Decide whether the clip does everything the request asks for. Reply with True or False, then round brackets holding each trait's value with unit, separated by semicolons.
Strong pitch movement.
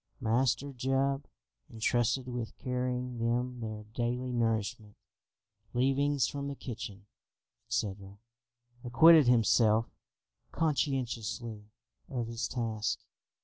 False (2.7 semitones)